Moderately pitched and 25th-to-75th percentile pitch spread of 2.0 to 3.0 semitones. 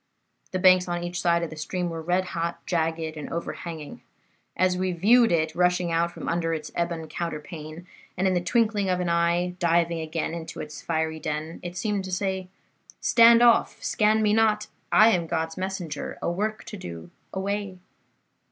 Yes: medium, 175 Hz; narrow, 2.5 semitones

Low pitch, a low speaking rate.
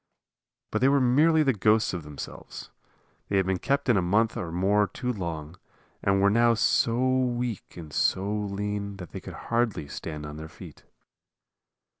No: low, 105 Hz; average, 175 wpm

